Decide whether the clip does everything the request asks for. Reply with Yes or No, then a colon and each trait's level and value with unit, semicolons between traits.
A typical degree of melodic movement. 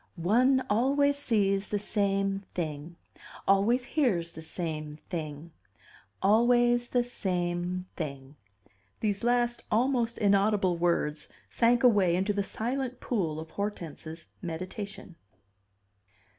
No: wide, 5.8 semitones